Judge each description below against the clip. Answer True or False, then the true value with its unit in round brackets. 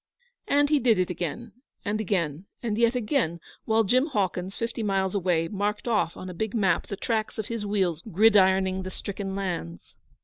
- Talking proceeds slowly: False (180 wpm)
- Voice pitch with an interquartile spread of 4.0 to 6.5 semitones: False (3.3 semitones)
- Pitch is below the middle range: False (200 Hz)